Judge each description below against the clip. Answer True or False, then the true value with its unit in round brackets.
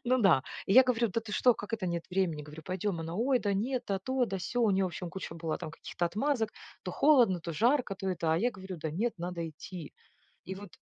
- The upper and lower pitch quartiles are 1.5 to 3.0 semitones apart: False (5.4 semitones)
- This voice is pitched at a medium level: False (195 Hz)